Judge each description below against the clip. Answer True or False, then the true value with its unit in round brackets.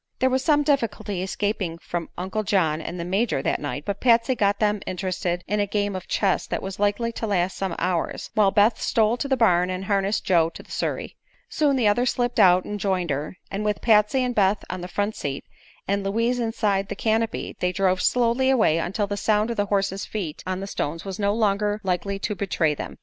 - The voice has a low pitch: False (200 Hz)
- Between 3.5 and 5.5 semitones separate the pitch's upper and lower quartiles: False (3.1 semitones)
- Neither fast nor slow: False (220 wpm)